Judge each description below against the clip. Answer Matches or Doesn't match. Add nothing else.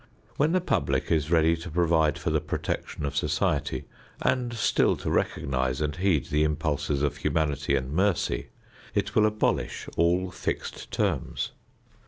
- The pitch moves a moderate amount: Matches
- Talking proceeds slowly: Doesn't match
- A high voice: Doesn't match